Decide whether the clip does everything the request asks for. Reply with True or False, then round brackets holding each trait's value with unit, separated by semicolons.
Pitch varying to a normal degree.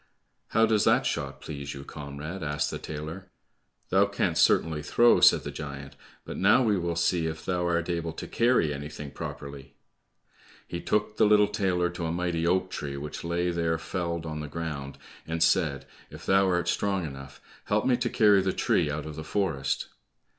True (4.1 semitones)